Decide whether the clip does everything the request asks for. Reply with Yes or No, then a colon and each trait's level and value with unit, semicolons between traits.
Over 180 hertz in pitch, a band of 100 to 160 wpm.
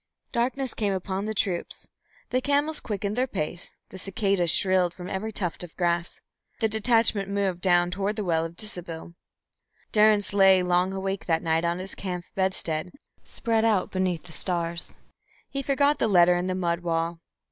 No: high, 190 Hz; average, 170 wpm